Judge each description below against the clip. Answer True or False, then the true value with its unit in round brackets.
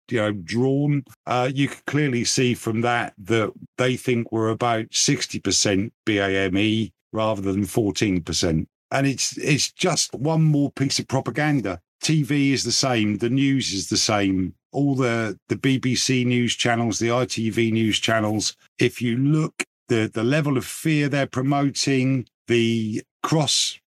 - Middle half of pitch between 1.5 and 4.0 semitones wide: True (3.7 semitones)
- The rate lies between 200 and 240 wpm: False (155 wpm)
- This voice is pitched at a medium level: False (120 Hz)